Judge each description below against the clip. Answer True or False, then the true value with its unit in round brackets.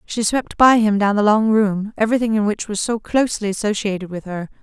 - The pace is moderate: False (220 wpm)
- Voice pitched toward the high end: True (210 Hz)